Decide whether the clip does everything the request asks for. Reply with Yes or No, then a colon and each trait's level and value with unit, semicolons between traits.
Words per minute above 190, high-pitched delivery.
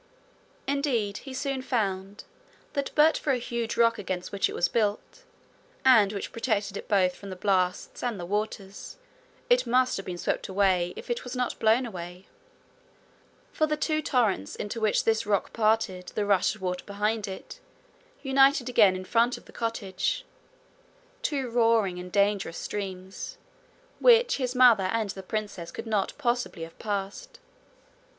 No: average, 160 wpm; high, 215 Hz